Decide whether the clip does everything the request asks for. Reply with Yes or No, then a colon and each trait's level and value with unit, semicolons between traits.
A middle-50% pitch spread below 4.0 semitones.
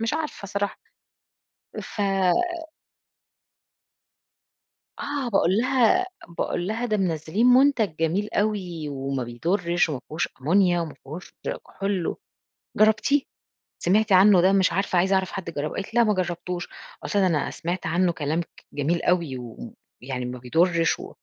No: average, 4.4 semitones